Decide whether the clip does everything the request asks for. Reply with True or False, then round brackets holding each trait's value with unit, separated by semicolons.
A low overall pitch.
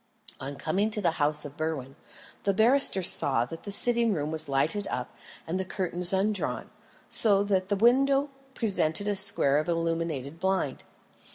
False (185 Hz)